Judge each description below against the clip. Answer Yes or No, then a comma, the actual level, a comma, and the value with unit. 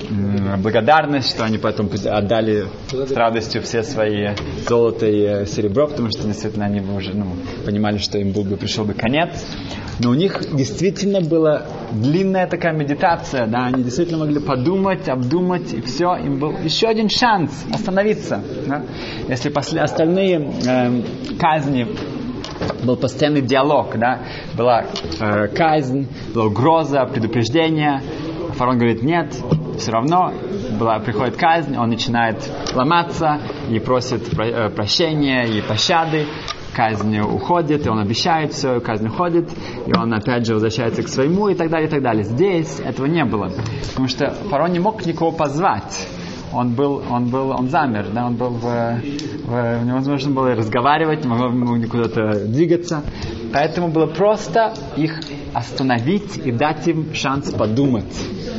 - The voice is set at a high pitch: No, low, 130 Hz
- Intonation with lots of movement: Yes, wide, 5.8 semitones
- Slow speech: No, average, 145 wpm